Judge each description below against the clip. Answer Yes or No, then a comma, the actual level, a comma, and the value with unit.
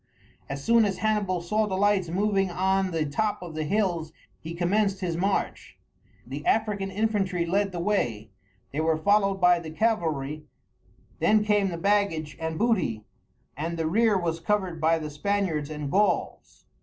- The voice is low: No, medium, 185 Hz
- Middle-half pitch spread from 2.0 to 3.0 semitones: No, average, 4.2 semitones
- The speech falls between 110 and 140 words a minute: No, average, 165 wpm